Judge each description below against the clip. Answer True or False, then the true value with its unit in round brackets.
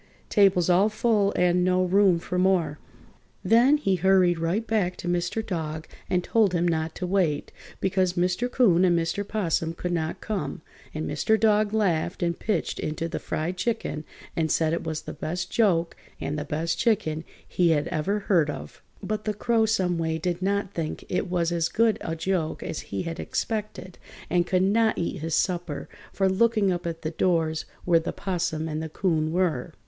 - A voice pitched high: False (180 Hz)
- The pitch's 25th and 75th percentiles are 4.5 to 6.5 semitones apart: False (3.4 semitones)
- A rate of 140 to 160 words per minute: False (190 wpm)